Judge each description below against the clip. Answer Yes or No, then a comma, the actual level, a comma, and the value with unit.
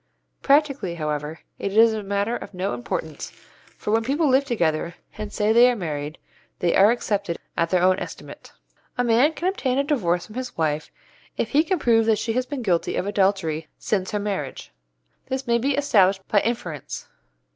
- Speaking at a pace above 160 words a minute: Yes, average, 190 wpm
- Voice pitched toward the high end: Yes, high, 210 Hz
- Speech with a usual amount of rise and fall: No, wide, 5.9 semitones